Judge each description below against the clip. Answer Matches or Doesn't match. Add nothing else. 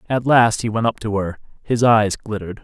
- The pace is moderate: Doesn't match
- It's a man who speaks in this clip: Matches